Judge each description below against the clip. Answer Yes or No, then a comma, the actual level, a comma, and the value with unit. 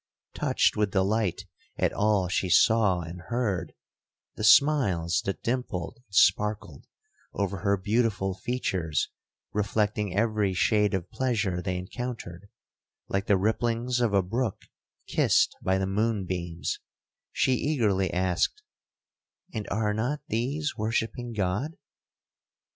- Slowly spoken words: Yes, slow, 115 wpm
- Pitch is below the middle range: Yes, low, 105 Hz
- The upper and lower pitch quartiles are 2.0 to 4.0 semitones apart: Yes, average, 3.6 semitones